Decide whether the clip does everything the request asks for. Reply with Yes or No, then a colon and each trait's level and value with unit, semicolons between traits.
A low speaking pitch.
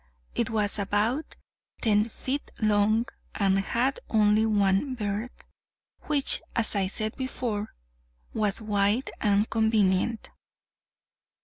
No: high, 215 Hz